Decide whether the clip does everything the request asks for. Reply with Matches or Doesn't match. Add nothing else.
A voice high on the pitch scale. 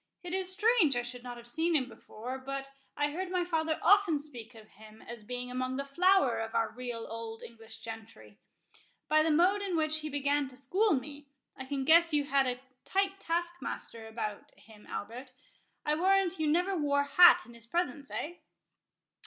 Matches